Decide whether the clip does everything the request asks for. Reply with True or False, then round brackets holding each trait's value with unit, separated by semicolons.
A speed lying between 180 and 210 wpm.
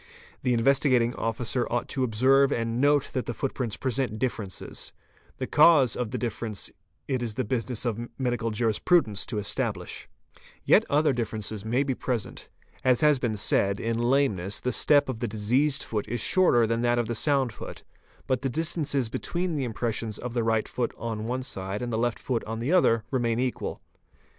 True (185 wpm)